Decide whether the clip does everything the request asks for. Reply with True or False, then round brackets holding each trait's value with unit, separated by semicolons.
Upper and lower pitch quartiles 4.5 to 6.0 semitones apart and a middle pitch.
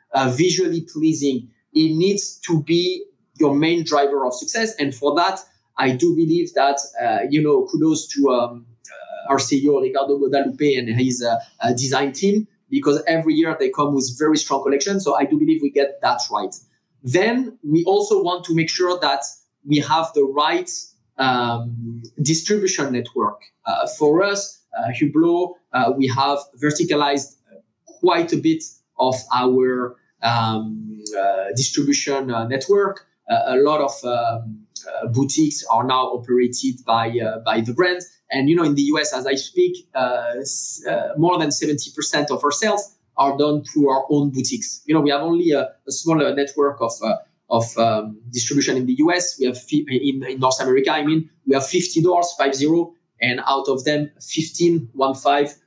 True (5.1 semitones; 145 Hz)